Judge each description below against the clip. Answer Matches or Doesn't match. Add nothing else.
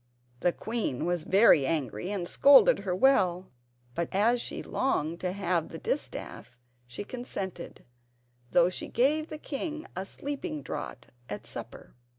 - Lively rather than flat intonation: Matches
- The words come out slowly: Doesn't match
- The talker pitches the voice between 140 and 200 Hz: Matches